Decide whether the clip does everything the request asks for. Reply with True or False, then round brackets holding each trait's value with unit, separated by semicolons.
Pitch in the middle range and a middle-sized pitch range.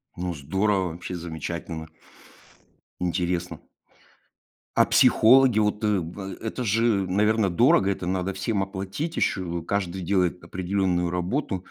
False (95 Hz; 3.0 semitones)